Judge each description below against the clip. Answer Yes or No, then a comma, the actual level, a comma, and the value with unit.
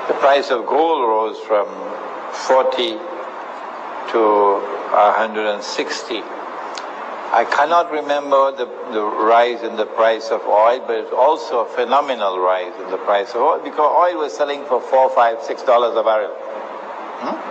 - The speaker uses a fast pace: No, average, 145 wpm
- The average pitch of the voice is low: Yes, low, 120 Hz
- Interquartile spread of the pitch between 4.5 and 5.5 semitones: Yes, average, 5.1 semitones